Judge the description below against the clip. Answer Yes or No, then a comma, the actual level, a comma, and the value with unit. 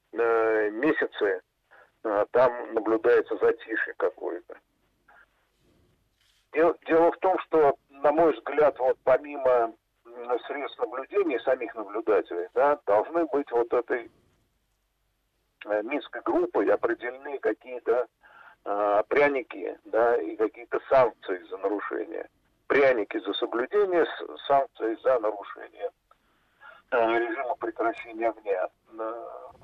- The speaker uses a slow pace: Yes, slow, 85 wpm